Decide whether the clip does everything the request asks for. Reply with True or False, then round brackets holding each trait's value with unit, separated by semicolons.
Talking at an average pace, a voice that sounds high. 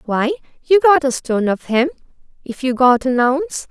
True (195 wpm; 275 Hz)